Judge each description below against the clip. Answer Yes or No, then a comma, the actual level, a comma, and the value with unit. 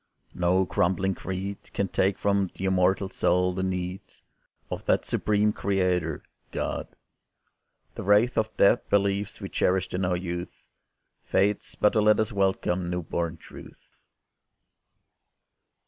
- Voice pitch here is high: No, very low, 95 Hz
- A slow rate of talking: Yes, slow, 130 wpm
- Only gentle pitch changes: Yes, narrow, 1.8 semitones